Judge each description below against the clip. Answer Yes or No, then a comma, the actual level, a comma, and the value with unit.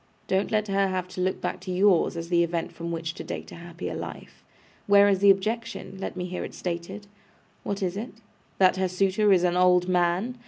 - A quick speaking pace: Yes, fast, 220 wpm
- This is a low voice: No, medium, 185 Hz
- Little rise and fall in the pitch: Yes, narrow, 2.2 semitones